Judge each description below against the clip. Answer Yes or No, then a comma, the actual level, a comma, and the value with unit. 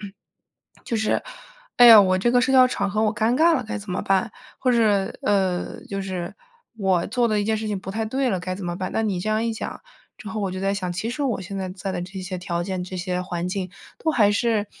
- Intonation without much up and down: No, average, 3.2 semitones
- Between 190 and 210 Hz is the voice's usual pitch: Yes, high, 200 Hz